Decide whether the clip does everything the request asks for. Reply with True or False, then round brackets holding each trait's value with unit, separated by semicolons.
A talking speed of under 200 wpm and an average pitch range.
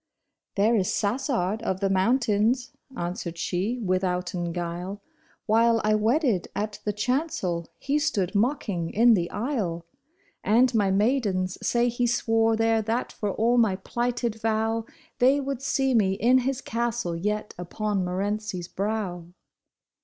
True (145 wpm; 4.1 semitones)